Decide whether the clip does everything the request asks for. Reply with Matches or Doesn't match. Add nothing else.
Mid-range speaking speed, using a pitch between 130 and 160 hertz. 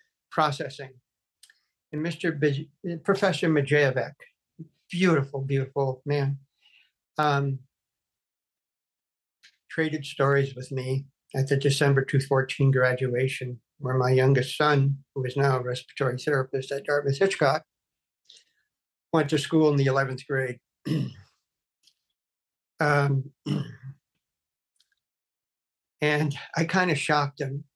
Doesn't match